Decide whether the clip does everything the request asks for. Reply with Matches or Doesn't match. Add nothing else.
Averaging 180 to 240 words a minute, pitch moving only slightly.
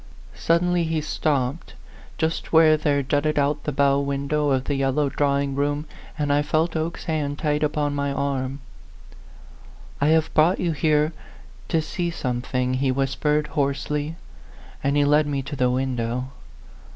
Doesn't match